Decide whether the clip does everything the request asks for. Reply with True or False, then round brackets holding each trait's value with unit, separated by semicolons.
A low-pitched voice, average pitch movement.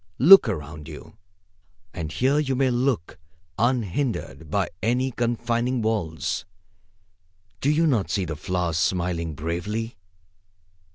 False (110 Hz; 7.2 semitones)